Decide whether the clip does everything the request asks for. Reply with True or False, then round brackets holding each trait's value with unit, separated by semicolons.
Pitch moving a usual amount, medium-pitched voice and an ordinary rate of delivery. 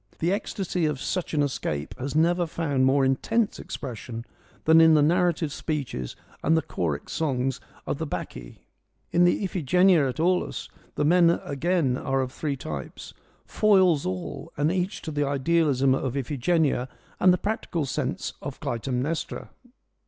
True (4.5 semitones; 150 Hz; 150 wpm)